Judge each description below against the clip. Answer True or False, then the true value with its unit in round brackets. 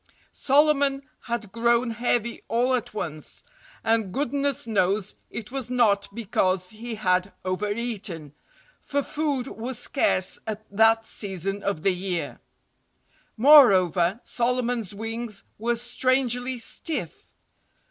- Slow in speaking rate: True (105 wpm)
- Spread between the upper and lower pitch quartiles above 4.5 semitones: False (4.0 semitones)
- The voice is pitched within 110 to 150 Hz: False (230 Hz)